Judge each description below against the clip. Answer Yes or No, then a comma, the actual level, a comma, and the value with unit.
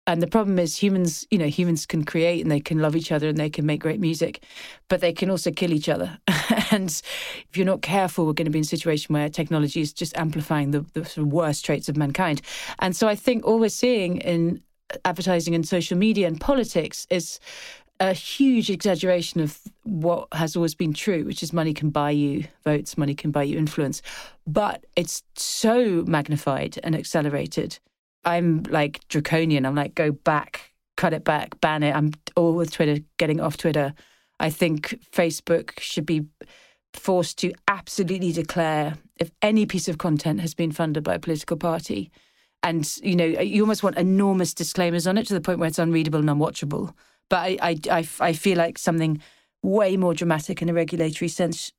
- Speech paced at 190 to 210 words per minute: Yes, average, 195 wpm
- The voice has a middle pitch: Yes, medium, 170 Hz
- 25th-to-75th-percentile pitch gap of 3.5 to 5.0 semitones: No, average, 3.0 semitones